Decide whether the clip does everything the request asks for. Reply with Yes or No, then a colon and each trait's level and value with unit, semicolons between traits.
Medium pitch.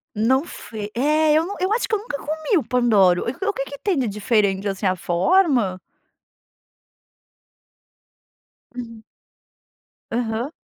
No: high, 245 Hz